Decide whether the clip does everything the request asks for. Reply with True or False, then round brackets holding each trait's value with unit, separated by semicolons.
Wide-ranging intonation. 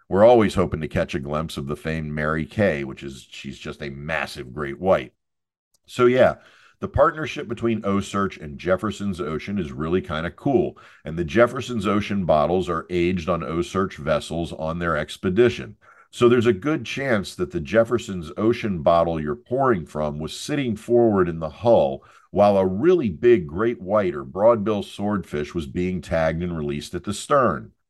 True (6.1 semitones)